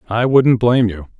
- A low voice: Yes, low, 115 Hz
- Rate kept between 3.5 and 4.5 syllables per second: No, 5.4 syllables/s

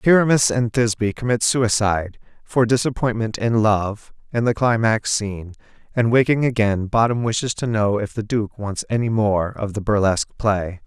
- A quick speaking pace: No, average, 165 wpm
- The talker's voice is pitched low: Yes, low, 110 Hz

